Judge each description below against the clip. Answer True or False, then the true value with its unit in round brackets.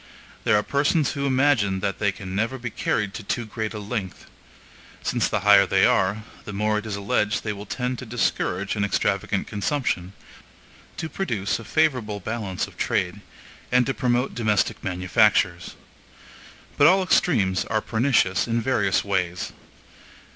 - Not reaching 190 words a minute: True (160 wpm)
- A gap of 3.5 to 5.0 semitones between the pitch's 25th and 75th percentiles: True (4.0 semitones)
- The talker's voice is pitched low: True (105 Hz)